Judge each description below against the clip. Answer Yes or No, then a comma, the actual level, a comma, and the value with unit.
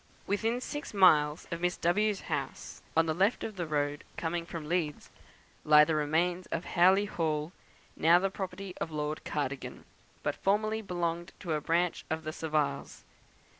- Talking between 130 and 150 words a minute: No, average, 170 wpm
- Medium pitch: Yes, medium, 170 Hz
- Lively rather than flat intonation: No, average, 3.6 semitones